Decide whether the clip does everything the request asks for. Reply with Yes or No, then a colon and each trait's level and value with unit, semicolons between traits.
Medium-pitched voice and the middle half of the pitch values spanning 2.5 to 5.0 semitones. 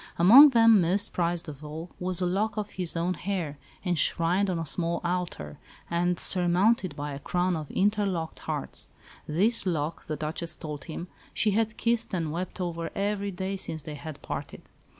Yes: medium, 175 Hz; average, 3.5 semitones